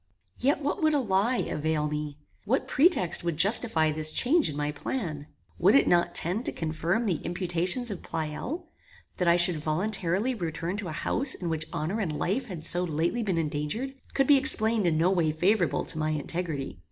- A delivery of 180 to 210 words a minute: Yes, average, 190 wpm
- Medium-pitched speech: Yes, medium, 175 Hz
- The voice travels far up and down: Yes, wide, 6.1 semitones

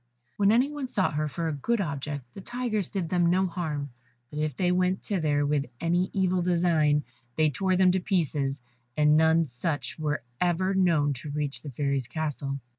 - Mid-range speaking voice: Yes, medium, 160 Hz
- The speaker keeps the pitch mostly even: No, average, 4.1 semitones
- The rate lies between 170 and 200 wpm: Yes, average, 190 wpm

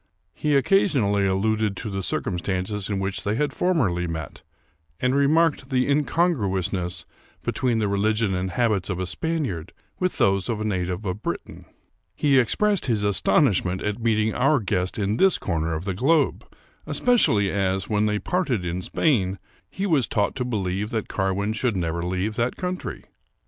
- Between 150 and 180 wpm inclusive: Yes, average, 170 wpm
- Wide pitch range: Yes, wide, 5.8 semitones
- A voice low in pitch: Yes, low, 105 Hz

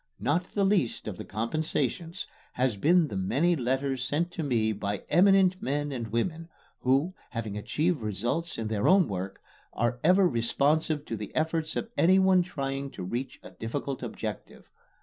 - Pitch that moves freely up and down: Yes, wide, 6.6 semitones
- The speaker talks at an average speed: Yes, average, 165 wpm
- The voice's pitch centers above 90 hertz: Yes, medium, 140 Hz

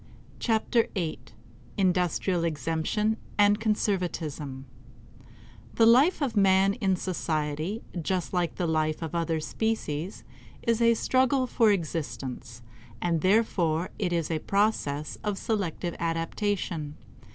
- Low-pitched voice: No, medium, 180 Hz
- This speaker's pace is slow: Yes, slow, 120 wpm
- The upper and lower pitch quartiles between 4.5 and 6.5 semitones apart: Yes, average, 4.9 semitones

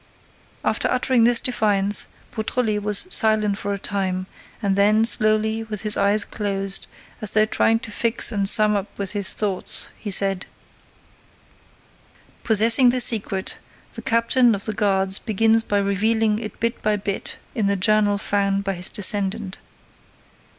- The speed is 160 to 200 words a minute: No, average, 150 wpm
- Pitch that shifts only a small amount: Yes, narrow, 2.0 semitones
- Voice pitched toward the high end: Yes, high, 210 Hz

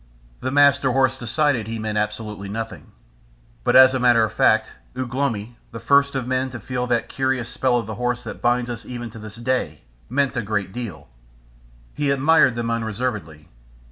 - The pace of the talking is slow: No, average, 185 wpm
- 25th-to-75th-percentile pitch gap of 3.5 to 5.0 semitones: No, average, 2.7 semitones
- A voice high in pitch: No, low, 120 Hz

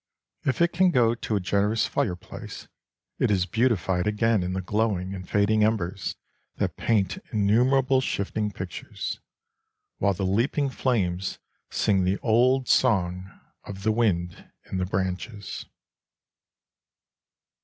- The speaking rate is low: Yes, slow, 125 wpm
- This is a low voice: Yes, low, 105 Hz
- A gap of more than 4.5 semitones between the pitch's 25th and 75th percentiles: No, average, 3.7 semitones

